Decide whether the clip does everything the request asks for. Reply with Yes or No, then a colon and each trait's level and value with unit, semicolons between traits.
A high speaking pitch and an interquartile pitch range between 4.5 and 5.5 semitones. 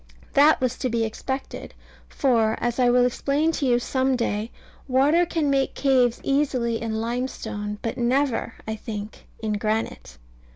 No: high, 245 Hz; average, 3.2 semitones